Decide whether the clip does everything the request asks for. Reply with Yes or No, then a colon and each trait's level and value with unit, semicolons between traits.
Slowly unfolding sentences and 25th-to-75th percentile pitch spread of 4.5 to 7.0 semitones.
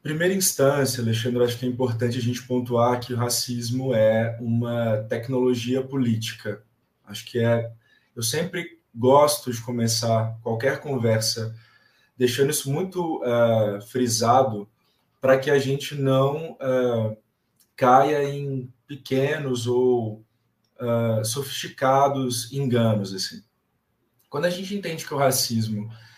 No: slow, 110 wpm; average, 3.0 semitones